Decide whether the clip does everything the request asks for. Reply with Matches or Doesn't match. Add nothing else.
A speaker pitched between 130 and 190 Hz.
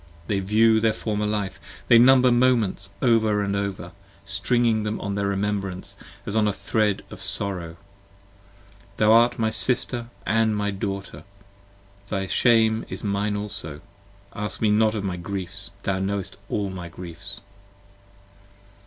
Doesn't match